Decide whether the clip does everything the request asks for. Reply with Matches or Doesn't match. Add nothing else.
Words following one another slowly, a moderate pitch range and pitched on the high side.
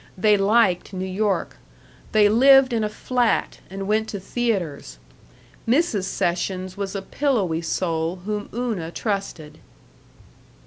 Matches